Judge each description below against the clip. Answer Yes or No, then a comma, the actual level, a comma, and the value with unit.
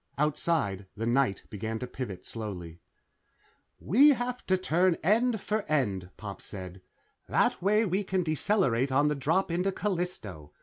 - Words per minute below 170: Yes, average, 145 wpm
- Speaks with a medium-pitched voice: Yes, medium, 150 Hz